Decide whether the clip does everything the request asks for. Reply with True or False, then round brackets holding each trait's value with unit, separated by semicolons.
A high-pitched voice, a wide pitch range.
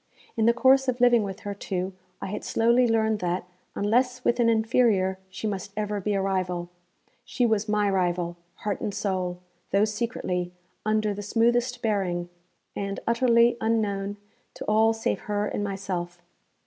False (210 Hz; 3.2 semitones)